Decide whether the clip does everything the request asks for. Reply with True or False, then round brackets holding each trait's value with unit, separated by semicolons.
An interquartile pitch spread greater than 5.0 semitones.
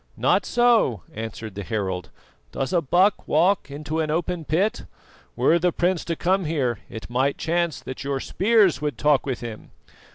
True (5.6 semitones)